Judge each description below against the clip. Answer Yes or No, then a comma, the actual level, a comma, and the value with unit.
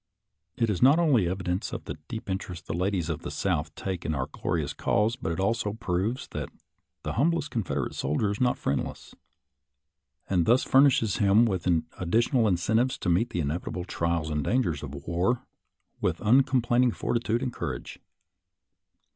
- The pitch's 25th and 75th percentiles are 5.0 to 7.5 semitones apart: Yes, wide, 5.6 semitones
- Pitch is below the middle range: Yes, low, 100 Hz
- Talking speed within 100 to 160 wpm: No, average, 170 wpm